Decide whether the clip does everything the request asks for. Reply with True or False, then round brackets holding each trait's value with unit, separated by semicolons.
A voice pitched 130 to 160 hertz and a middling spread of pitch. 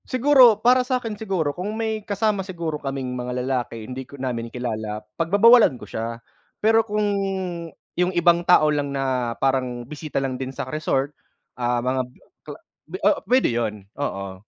False (140 Hz; 8.6 semitones)